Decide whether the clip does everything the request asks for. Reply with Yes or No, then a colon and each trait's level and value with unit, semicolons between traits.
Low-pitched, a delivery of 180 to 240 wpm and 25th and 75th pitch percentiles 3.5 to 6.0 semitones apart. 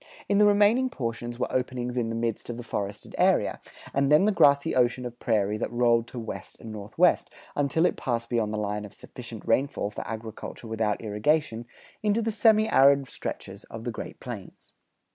Yes: low, 120 Hz; average, 190 wpm; average, 4.2 semitones